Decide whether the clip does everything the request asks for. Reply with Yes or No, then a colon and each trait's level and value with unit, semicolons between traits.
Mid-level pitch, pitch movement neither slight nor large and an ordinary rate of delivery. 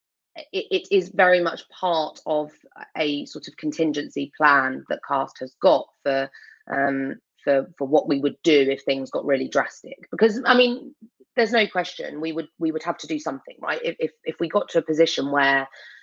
Yes: medium, 160 Hz; average, 4.5 semitones; average, 190 wpm